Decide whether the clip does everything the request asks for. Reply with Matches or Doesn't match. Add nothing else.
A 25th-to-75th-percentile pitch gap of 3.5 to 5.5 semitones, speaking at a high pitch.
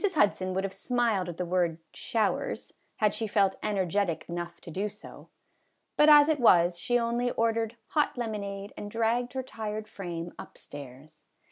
Matches